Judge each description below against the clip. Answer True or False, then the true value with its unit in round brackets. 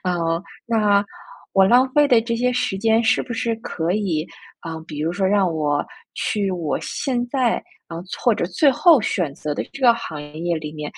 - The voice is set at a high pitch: True (195 Hz)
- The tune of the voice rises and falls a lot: True (6.0 semitones)